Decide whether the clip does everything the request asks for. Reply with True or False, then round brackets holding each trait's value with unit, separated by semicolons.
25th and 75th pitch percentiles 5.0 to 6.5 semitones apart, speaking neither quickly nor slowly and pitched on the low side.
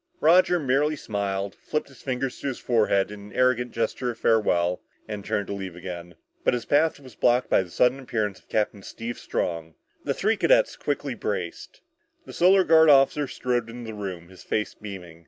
True (5.4 semitones; 190 wpm; 115 Hz)